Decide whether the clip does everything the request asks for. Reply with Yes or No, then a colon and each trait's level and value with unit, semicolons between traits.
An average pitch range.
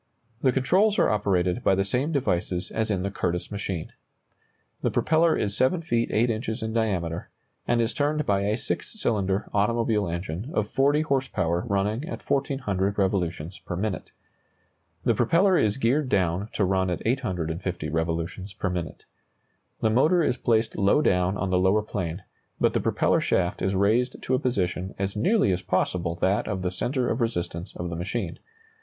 Yes: average, 5.0 semitones